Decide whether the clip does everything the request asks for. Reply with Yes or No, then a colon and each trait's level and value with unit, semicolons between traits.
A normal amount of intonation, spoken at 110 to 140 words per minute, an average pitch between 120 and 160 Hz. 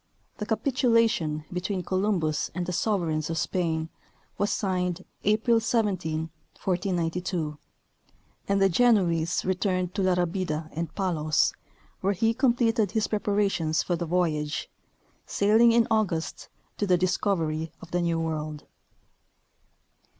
No: average, 4.0 semitones; slow, 135 wpm; medium, 180 Hz